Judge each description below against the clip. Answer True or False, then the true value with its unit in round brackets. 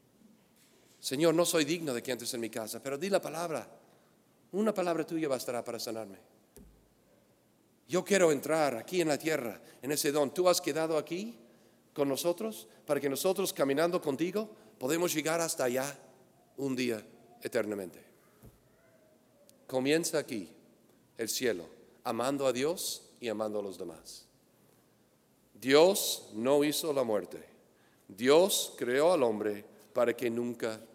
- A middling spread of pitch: False (5.7 semitones)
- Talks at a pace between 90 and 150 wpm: True (140 wpm)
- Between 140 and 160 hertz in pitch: True (145 Hz)